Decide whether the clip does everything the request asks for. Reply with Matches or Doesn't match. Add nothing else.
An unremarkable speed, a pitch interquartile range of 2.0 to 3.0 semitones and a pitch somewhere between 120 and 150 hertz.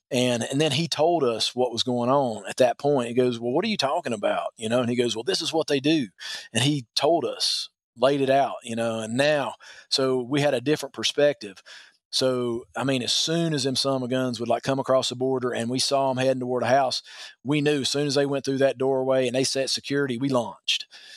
Doesn't match